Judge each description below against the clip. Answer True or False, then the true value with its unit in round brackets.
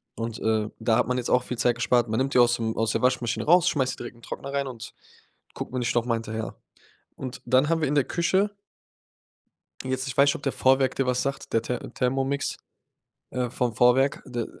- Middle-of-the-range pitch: False (125 Hz)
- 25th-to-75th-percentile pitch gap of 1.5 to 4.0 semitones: True (2.5 semitones)